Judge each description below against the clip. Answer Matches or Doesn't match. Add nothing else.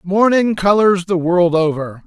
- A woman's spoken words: Doesn't match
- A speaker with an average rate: Matches